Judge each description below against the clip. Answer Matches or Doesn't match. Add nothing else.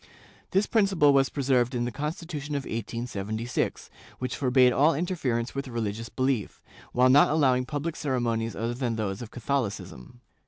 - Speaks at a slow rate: Doesn't match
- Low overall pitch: Matches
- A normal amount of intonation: Matches